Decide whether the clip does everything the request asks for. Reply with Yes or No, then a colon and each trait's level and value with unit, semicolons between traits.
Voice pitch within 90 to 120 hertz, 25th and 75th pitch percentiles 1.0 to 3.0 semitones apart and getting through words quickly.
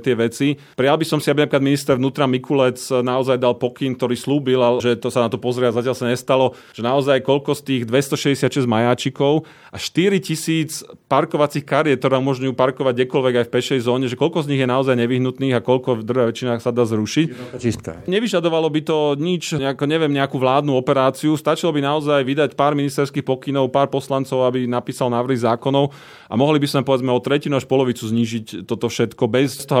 No: low, 135 Hz; narrow, 2.4 semitones; fast, 195 wpm